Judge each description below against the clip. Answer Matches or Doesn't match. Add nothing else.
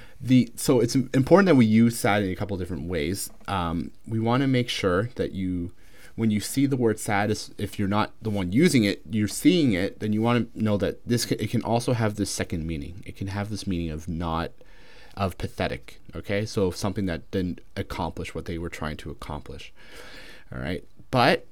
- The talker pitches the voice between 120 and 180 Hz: Doesn't match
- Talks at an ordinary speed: Doesn't match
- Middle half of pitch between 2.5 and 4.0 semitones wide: Doesn't match